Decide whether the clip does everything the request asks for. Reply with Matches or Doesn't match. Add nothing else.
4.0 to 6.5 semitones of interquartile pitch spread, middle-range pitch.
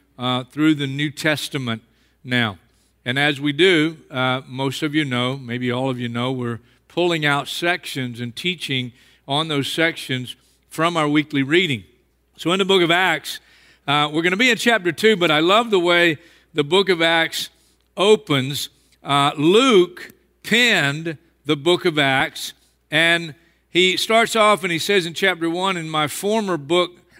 Matches